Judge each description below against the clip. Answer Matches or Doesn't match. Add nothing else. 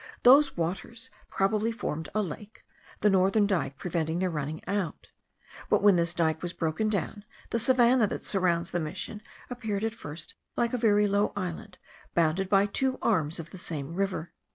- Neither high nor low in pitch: Doesn't match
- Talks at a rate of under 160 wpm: Doesn't match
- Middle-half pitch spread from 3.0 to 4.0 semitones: Doesn't match